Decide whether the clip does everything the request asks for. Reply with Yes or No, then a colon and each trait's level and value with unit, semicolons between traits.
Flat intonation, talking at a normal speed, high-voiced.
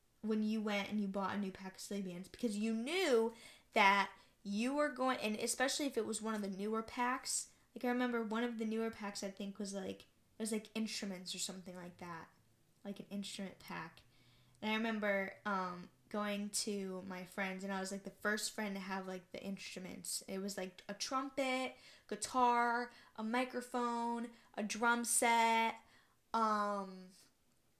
No: average, 3.2 semitones; average, 180 wpm; high, 210 Hz